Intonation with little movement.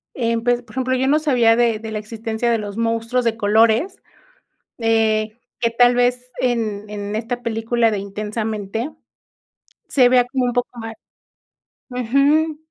Yes: narrow, 2.0 semitones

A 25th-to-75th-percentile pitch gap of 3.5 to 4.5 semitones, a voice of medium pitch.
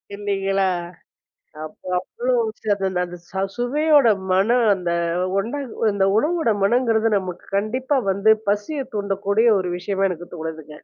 No: average, 4.1 semitones; high, 200 Hz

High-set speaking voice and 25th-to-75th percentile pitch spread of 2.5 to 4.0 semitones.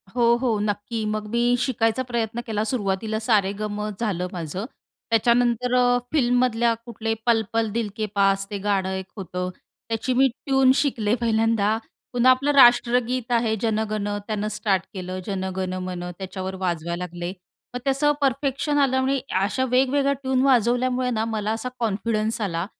Yes: high, 225 Hz; average, 3.6 semitones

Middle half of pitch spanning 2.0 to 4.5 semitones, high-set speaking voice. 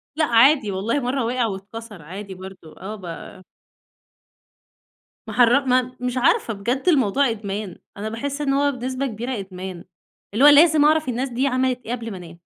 No: average, 5.0 semitones; high, 235 Hz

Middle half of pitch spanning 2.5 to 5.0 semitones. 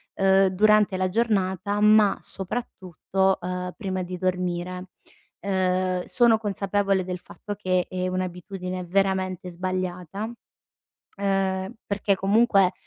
No: narrow, 1.5 semitones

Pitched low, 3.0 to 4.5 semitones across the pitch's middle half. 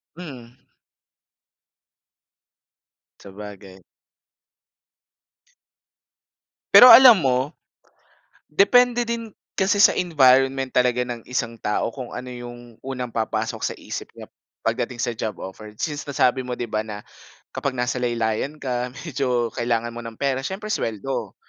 Yes: low, 125 Hz; average, 3.4 semitones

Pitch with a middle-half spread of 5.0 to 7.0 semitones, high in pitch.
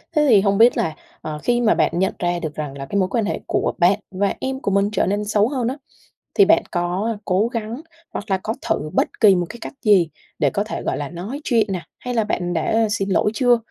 No: average, 4.2 semitones; high, 205 Hz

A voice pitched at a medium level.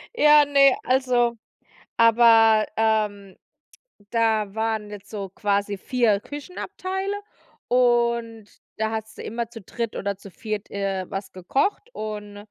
No: high, 220 Hz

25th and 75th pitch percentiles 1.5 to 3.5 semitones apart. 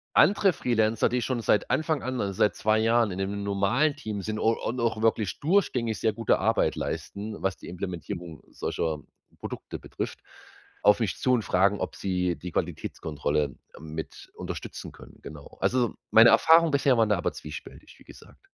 No: average, 4.7 semitones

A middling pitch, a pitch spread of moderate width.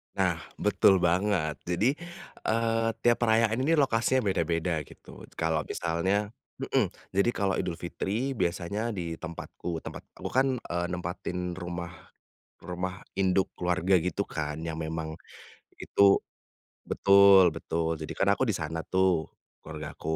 No: very low, 90 Hz; average, 3.5 semitones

